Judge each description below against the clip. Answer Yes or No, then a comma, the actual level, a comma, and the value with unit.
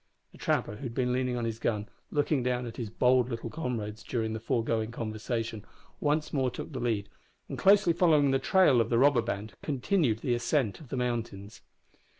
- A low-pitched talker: Yes, low, 120 Hz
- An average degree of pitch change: Yes, average, 3.4 semitones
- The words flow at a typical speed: Yes, average, 195 wpm